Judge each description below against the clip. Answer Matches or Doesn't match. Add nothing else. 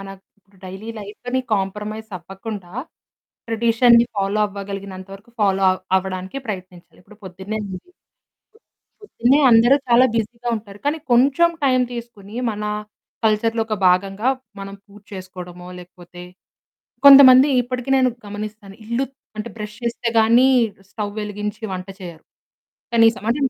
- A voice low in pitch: Doesn't match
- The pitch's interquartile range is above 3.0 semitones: Matches